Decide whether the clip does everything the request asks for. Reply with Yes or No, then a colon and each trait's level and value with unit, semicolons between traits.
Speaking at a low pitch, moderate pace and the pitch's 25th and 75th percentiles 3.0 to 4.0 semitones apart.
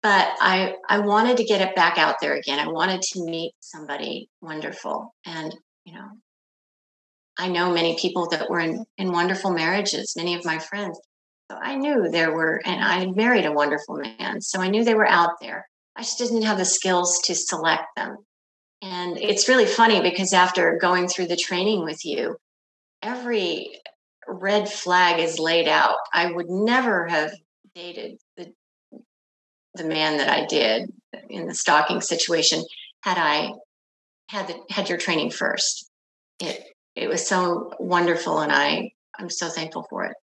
No: medium, 180 Hz; average, 170 wpm; average, 3.7 semitones